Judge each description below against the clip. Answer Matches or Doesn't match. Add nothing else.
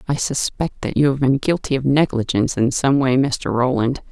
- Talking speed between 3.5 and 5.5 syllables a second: Matches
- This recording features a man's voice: Doesn't match